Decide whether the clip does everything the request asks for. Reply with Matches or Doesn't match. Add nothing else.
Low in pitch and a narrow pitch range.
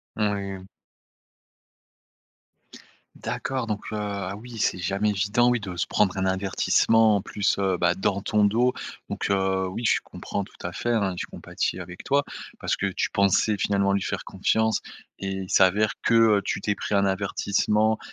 Matches